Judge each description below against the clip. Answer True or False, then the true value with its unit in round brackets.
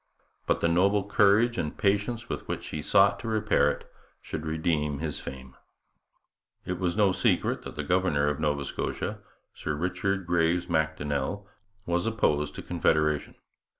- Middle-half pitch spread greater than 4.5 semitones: True (4.9 semitones)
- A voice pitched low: True (85 Hz)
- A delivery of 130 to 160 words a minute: True (150 wpm)